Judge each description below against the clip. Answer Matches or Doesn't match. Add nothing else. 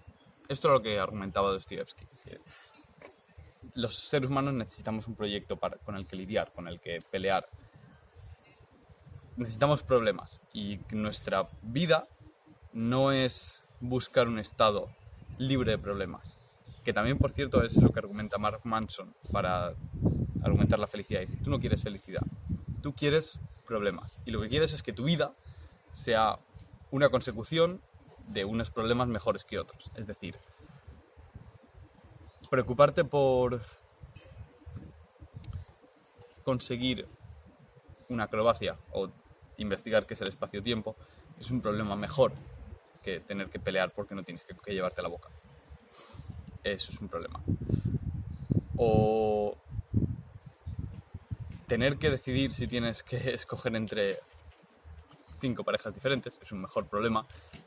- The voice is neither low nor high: Doesn't match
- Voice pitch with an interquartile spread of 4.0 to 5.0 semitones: Matches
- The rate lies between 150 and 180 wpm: Doesn't match